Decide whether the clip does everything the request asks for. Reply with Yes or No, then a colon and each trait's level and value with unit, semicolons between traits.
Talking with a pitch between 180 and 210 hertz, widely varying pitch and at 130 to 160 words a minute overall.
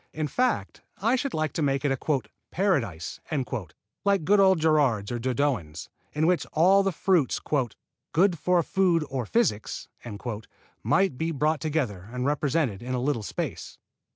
No: medium, 155 Hz; wide, 6.1 semitones; average, 155 wpm